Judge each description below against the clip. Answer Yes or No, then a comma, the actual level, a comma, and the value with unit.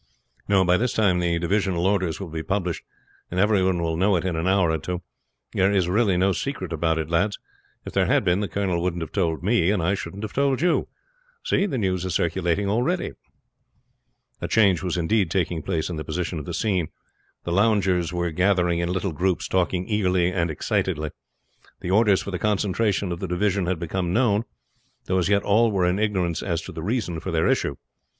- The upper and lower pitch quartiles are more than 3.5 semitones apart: No, average, 2.8 semitones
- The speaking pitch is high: No, very low, 90 Hz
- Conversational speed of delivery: No, fast, 210 wpm